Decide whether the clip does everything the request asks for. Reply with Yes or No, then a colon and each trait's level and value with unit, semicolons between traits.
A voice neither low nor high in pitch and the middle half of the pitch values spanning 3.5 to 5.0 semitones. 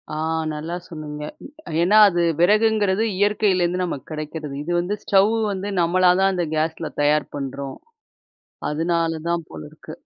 Yes: medium, 170 Hz; average, 3.8 semitones